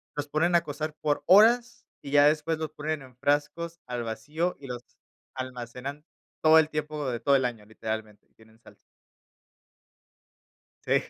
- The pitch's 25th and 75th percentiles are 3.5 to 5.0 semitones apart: Yes, average, 4.1 semitones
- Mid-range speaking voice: Yes, medium, 145 Hz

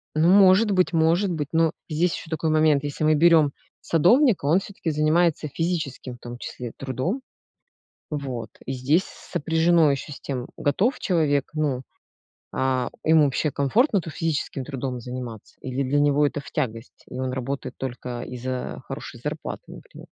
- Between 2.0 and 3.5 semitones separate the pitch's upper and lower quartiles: No, average, 4.0 semitones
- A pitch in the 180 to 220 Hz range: No, medium, 150 Hz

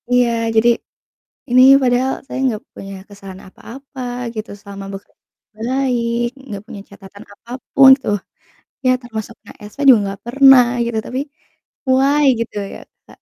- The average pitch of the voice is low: No, high, 235 Hz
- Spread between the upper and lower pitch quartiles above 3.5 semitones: Yes, average, 4.1 semitones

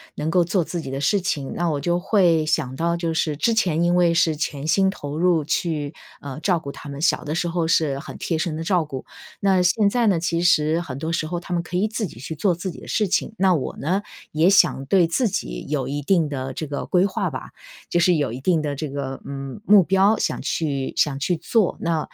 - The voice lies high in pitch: No, medium, 165 Hz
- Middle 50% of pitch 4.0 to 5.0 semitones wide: No, average, 3.6 semitones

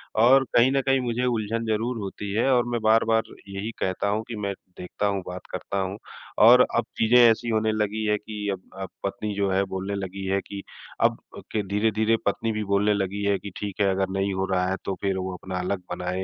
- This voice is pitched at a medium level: No, low, 105 Hz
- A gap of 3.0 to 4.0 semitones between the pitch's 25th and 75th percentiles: No, narrow, 2.5 semitones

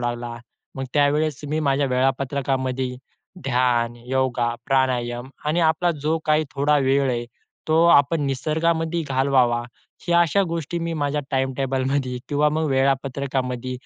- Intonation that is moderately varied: Yes, average, 3.1 semitones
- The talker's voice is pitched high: No, low, 135 Hz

